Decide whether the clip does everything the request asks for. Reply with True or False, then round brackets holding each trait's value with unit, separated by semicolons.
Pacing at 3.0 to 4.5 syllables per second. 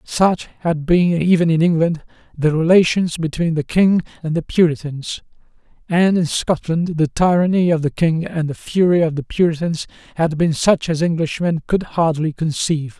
False (4.7 syllables/s)